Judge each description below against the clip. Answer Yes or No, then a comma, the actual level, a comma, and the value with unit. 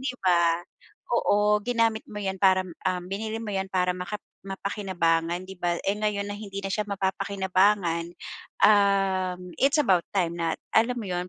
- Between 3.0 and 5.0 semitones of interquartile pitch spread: No, narrow, 2.4 semitones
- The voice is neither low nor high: No, high, 195 Hz